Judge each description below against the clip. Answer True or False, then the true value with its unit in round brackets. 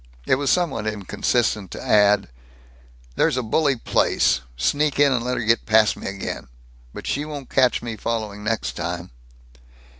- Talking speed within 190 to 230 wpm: False (160 wpm)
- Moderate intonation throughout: True (4.3 semitones)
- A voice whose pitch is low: True (115 Hz)